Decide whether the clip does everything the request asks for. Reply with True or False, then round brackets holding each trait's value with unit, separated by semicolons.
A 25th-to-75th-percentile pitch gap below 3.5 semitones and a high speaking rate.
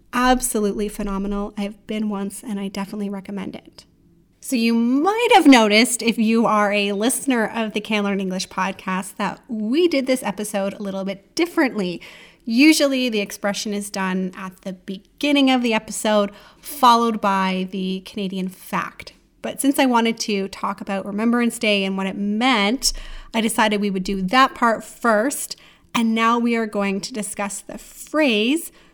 False (3.1 semitones; 165 wpm)